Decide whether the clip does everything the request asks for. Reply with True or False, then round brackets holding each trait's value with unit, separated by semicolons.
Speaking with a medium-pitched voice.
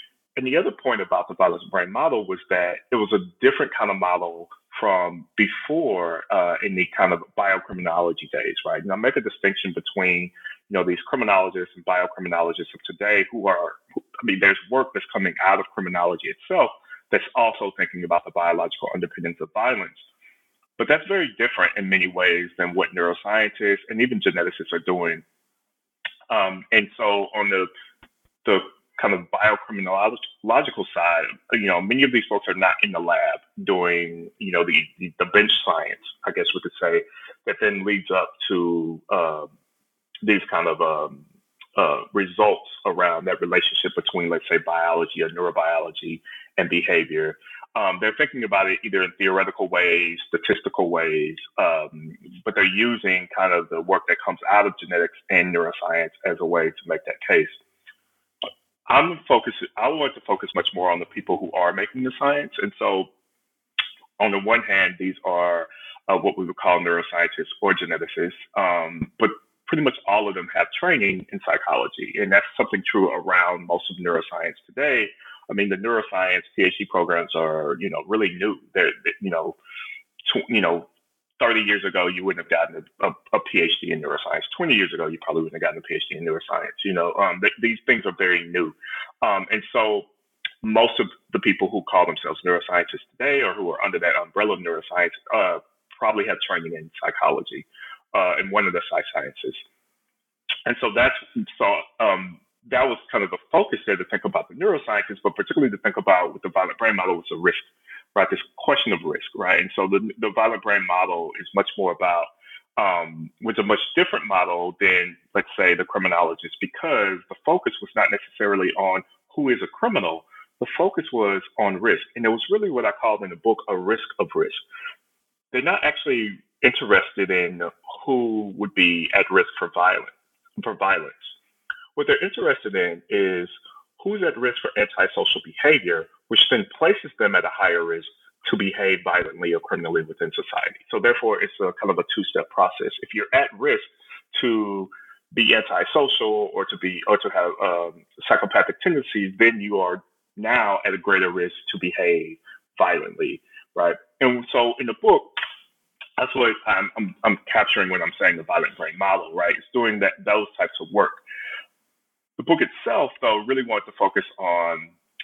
False (120 Hz)